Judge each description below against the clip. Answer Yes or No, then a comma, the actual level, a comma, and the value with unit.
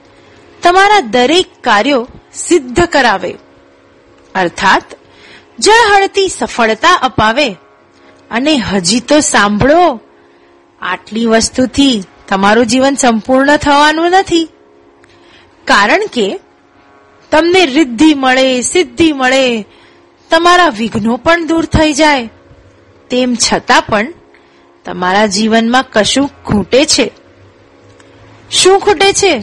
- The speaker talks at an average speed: Yes, average, 90 wpm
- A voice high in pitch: Yes, very high, 260 Hz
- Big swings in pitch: Yes, wide, 7.2 semitones